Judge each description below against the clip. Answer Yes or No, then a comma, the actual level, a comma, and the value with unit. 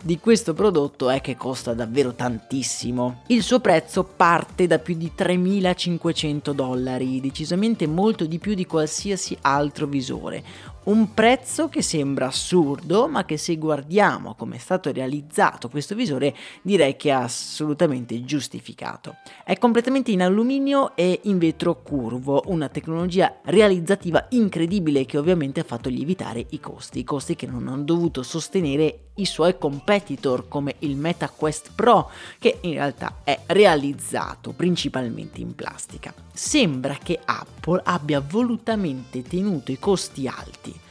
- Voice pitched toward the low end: No, medium, 160 Hz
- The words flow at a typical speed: Yes, average, 140 wpm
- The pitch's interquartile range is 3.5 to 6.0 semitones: Yes, wide, 5.4 semitones